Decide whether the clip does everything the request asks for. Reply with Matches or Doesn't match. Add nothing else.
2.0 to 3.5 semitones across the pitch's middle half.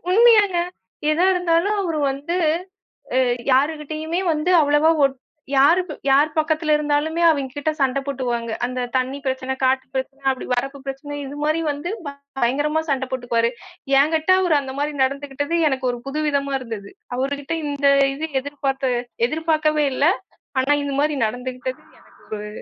Matches